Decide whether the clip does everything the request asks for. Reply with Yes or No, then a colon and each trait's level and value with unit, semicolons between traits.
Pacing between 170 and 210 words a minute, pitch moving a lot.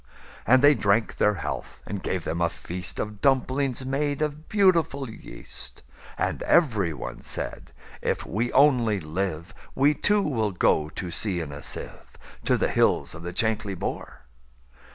No: average, 145 wpm; wide, 7.6 semitones